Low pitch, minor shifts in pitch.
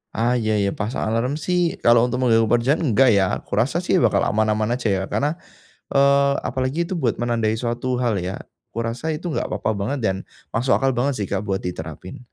No: low, 120 Hz; average, 4.2 semitones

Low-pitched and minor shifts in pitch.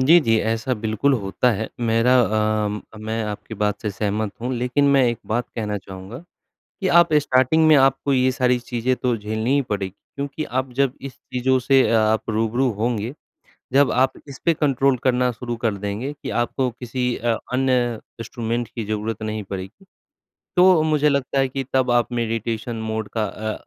No: low, 120 Hz; average, 3.3 semitones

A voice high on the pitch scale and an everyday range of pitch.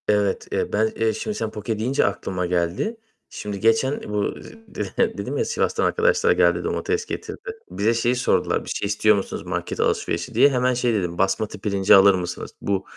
No: low, 105 Hz; average, 4.2 semitones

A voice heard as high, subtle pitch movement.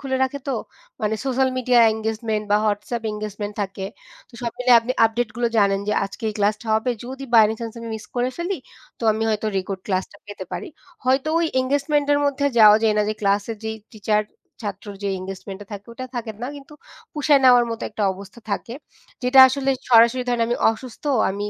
No: high, 225 Hz; average, 3.6 semitones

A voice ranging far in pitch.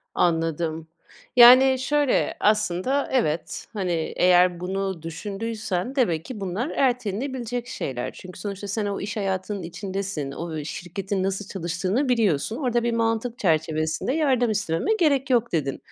Yes: wide, 5.7 semitones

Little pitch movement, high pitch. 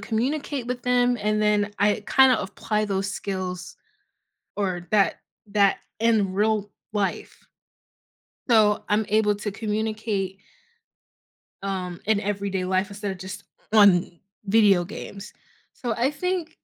Yes: narrow, 2.2 semitones; high, 210 Hz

